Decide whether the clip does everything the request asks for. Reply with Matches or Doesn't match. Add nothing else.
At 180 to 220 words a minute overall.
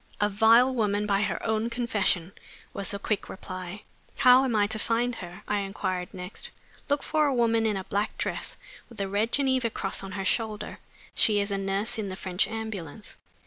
Matches